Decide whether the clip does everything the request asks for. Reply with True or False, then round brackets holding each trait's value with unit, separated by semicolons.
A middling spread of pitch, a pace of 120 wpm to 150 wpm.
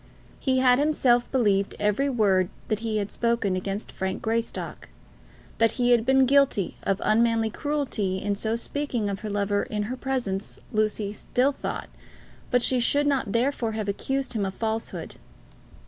False (4.0 semitones; 165 wpm)